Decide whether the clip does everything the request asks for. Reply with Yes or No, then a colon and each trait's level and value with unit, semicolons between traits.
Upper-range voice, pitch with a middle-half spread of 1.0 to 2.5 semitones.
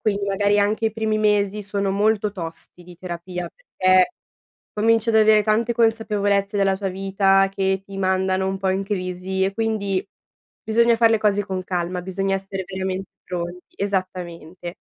Yes: high, 195 Hz; narrow, 2.0 semitones